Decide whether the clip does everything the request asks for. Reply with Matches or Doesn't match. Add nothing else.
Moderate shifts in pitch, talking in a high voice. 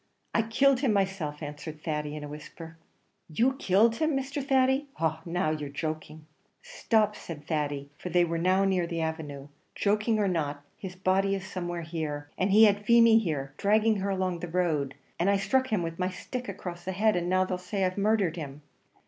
Doesn't match